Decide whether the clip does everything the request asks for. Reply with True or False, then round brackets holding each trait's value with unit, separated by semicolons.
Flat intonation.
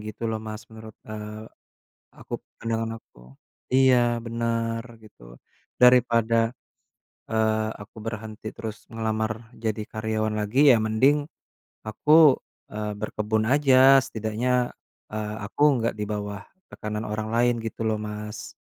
True (1.5 semitones)